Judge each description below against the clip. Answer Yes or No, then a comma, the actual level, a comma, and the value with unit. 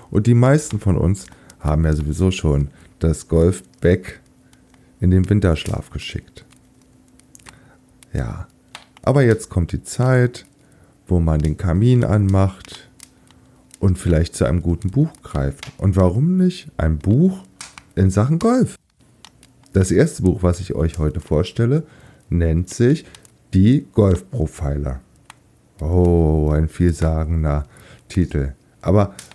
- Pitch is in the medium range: No, very low, 90 Hz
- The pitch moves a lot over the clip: Yes, wide, 6.5 semitones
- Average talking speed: No, slow, 120 wpm